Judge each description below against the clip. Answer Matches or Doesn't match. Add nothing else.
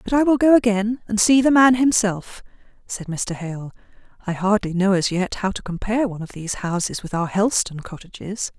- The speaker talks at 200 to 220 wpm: Matches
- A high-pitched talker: Matches